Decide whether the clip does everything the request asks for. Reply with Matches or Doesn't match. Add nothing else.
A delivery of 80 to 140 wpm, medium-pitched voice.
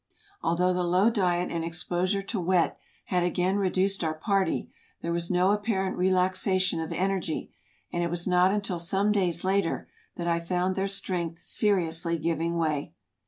Doesn't match